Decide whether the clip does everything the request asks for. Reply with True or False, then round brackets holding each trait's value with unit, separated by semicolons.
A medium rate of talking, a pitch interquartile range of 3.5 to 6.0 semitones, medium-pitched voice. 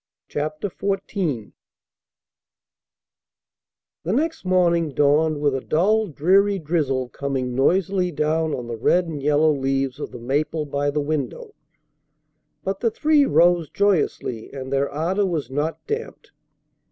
False (130 wpm; 4.9 semitones; 155 Hz)